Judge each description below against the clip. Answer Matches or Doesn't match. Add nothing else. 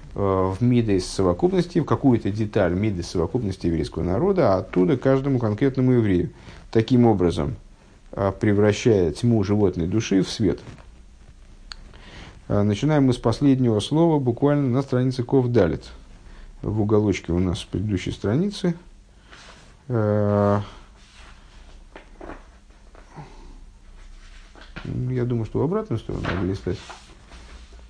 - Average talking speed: Doesn't match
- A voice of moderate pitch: Doesn't match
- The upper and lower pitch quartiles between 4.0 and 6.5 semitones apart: Matches